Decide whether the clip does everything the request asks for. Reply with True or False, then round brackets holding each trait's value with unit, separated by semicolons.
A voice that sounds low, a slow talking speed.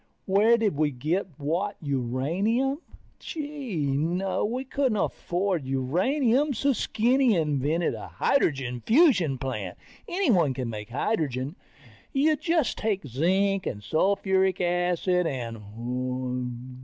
False (175 Hz; 110 wpm)